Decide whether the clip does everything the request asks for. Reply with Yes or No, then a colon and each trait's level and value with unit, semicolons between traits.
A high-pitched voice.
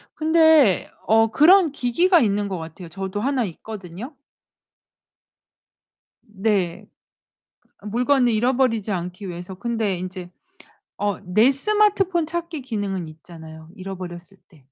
Yes: high, 210 Hz